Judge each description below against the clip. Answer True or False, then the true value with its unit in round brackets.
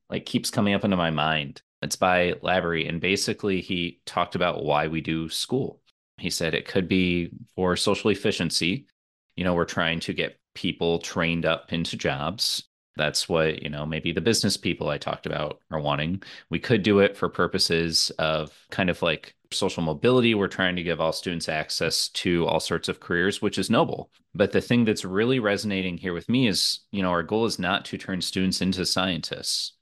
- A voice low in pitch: True (90 Hz)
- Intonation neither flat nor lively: True (3.1 semitones)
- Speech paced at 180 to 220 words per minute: True (200 wpm)